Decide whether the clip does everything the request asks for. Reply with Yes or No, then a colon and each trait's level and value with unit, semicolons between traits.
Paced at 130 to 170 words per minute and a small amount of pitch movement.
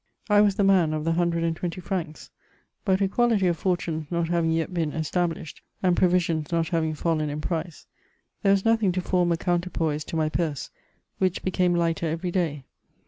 No: average, 185 wpm; narrow, 2.3 semitones